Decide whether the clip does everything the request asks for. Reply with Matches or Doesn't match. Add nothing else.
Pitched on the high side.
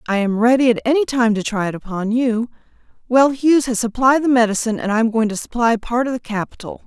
Matches